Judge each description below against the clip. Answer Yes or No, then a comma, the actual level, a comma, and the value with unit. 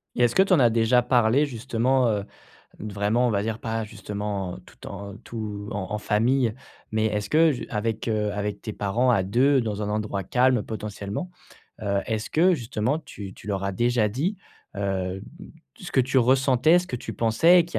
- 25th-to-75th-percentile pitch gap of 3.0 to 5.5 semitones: Yes, average, 3.8 semitones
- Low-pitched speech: Yes, low, 110 Hz